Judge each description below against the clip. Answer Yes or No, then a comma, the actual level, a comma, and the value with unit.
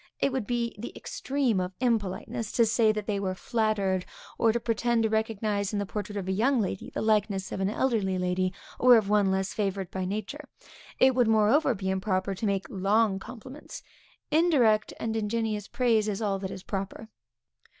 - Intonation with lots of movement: No, average, 3.0 semitones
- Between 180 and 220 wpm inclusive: Yes, average, 190 wpm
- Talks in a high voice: Yes, high, 215 Hz